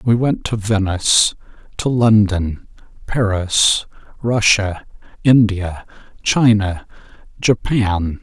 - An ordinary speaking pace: No, slow, 75 wpm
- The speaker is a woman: No, male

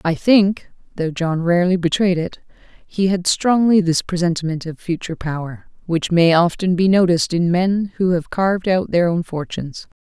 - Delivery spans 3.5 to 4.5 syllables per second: No, 5.0 syllables/s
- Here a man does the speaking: No, female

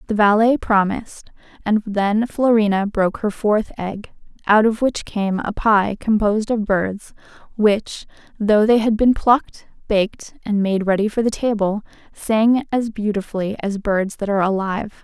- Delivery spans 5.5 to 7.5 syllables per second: No, 4.6 syllables/s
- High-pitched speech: Yes, high, 210 Hz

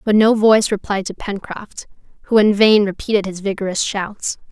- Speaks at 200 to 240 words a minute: No, average, 175 wpm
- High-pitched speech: Yes, high, 205 Hz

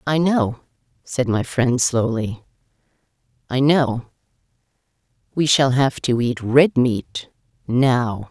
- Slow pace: Yes, slow, 100 wpm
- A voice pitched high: No, low, 125 Hz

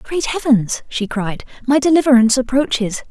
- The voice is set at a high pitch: Yes, very high, 250 Hz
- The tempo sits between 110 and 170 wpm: Yes, slow, 135 wpm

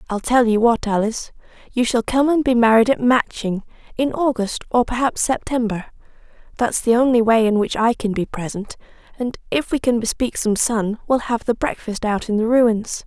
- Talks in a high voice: Yes, high, 230 Hz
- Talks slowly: No, average, 195 wpm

